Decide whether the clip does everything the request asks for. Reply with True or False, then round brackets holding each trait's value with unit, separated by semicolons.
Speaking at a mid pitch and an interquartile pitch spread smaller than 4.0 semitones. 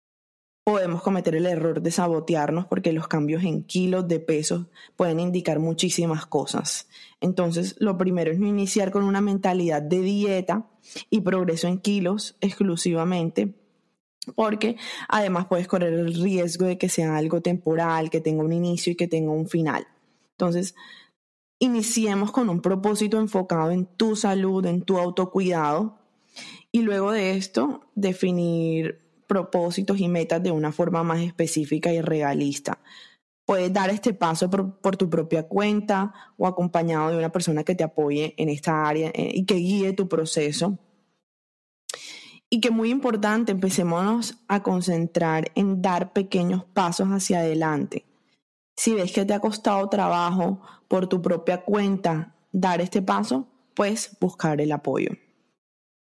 True (180 Hz; 3.2 semitones)